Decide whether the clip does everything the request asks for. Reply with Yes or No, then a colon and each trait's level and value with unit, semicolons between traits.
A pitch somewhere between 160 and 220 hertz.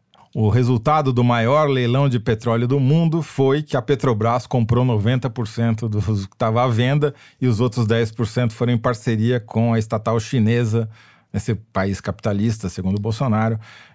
No: low, 120 Hz